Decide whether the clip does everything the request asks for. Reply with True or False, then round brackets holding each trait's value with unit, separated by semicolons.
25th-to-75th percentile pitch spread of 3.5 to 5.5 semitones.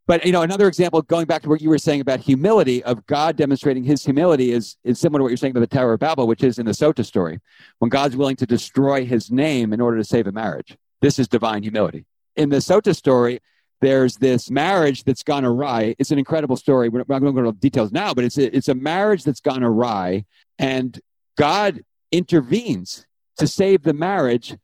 True (3.9 semitones)